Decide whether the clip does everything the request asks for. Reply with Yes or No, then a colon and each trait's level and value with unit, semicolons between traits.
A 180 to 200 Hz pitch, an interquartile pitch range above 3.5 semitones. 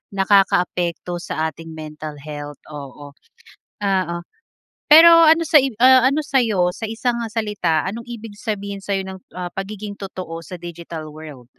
Yes: high, 190 Hz; average, 5.2 semitones